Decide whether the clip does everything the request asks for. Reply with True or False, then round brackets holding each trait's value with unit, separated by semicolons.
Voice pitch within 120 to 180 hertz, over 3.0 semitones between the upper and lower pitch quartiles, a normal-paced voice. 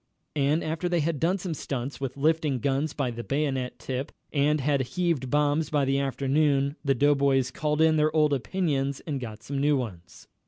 False (140 Hz; 2.4 semitones; 190 wpm)